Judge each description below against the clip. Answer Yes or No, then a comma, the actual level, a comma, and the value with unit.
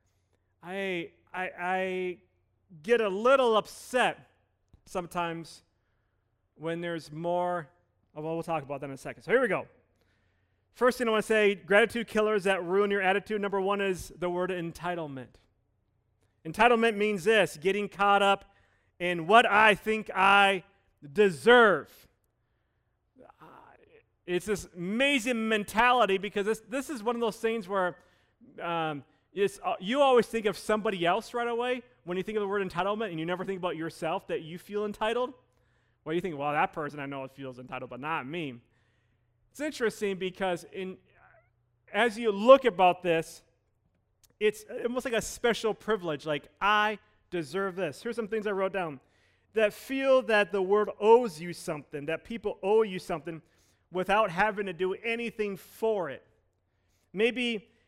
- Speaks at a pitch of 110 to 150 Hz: No, medium, 185 Hz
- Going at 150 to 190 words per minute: Yes, average, 160 wpm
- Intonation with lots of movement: Yes, wide, 6.5 semitones